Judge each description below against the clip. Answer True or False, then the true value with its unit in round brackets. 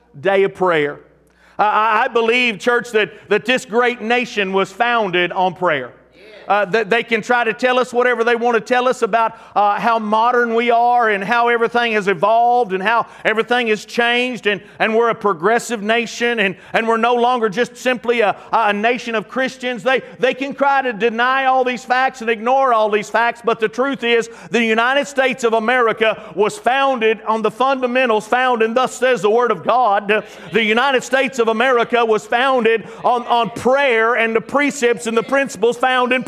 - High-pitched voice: True (235 Hz)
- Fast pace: False (195 wpm)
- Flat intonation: True (2.3 semitones)